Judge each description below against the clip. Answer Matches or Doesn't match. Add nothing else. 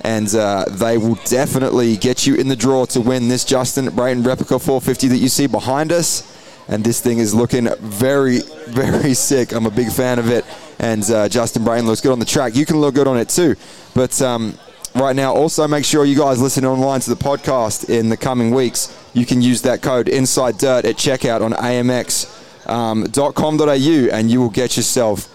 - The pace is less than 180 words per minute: Doesn't match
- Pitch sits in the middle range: Doesn't match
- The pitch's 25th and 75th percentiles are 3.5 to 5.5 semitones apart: Doesn't match